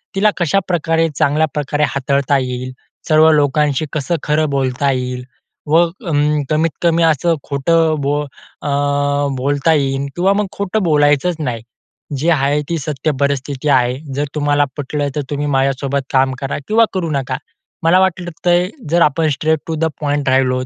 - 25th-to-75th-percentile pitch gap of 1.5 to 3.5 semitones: Yes, average, 3.0 semitones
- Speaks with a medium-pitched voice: Yes, medium, 150 Hz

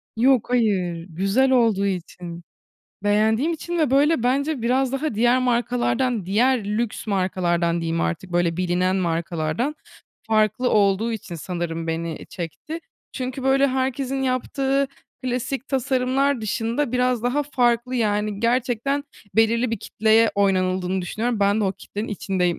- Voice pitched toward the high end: Yes, high, 225 Hz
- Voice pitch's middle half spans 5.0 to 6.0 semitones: Yes, wide, 5.5 semitones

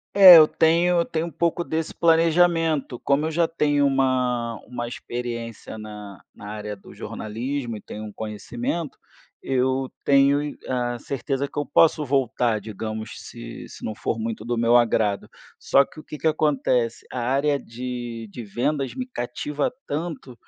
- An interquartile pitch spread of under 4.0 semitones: No, average, 4.6 semitones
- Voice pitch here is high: No, low, 130 Hz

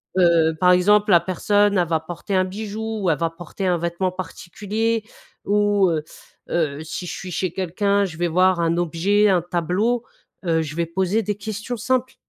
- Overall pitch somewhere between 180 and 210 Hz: Yes, medium, 185 Hz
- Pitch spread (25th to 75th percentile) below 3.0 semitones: No, average, 3.3 semitones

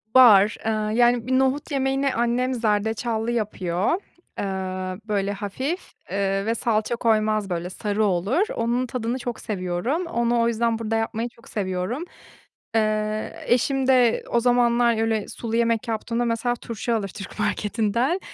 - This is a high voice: Yes, high, 230 Hz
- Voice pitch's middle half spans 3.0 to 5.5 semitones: No, narrow, 2.4 semitones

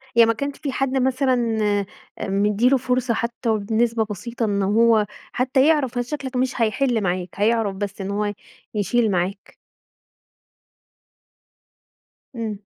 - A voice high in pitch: Yes, high, 230 Hz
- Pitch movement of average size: Yes, average, 3.6 semitones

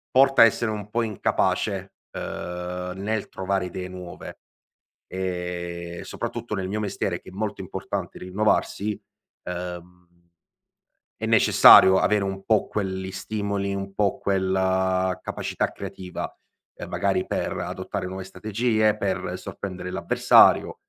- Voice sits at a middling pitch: No, very low, 95 Hz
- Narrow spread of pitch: Yes, narrow, 2.0 semitones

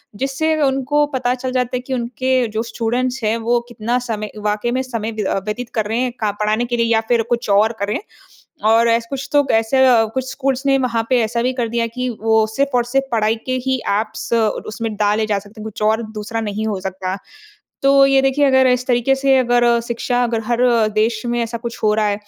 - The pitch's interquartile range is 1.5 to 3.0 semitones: Yes, average, 2.7 semitones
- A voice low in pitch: No, high, 235 Hz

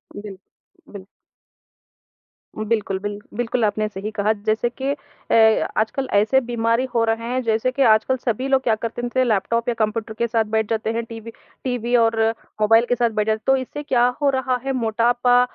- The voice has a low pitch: No, high, 230 Hz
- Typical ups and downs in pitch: No, narrow, 2.2 semitones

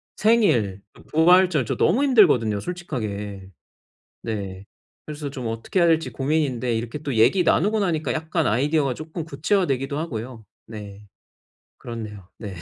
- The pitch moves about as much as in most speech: No, wide, 6.9 semitones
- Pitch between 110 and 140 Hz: Yes, low, 135 Hz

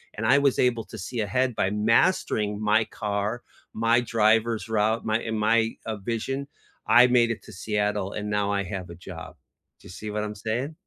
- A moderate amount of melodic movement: No, narrow, 2.0 semitones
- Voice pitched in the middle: No, low, 110 Hz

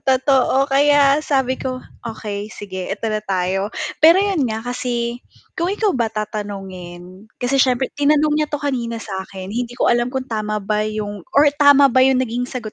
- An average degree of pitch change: Yes, average, 4.5 semitones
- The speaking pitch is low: No, high, 245 Hz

